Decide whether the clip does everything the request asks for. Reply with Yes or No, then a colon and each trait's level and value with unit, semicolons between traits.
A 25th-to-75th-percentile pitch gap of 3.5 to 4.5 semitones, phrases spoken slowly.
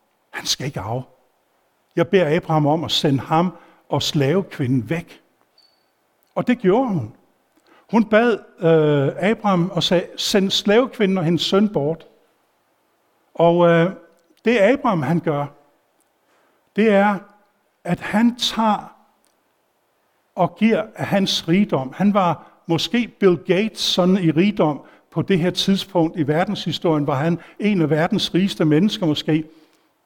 Yes: average, 4.2 semitones; slow, 135 wpm